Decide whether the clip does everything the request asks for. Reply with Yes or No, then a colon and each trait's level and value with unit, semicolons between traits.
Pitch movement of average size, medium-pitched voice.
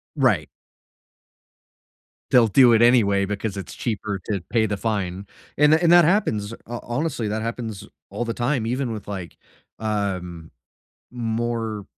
No: average, 3.1 semitones; low, 110 Hz